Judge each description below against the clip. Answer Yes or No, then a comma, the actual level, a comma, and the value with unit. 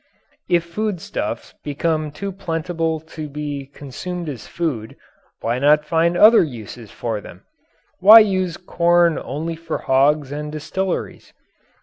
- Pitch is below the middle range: No, medium, 160 Hz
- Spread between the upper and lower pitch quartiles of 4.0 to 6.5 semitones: No, average, 3.3 semitones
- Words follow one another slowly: Yes, slow, 125 wpm